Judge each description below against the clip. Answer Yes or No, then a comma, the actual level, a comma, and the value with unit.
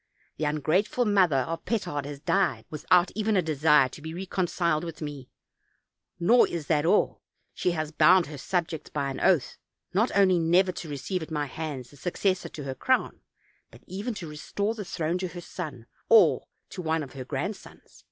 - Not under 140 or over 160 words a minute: No, average, 185 wpm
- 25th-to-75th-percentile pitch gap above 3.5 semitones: Yes, average, 4.1 semitones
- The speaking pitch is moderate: Yes, medium, 165 Hz